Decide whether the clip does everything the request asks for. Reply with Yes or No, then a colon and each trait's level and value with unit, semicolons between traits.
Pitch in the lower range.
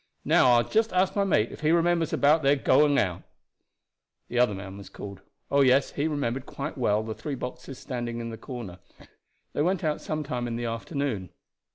Yes: low, 130 Hz